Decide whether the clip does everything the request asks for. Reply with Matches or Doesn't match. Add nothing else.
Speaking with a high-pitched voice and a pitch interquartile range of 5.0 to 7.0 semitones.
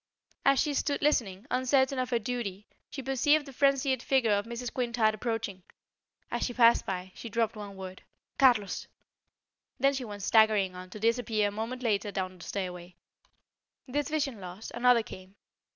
Doesn't match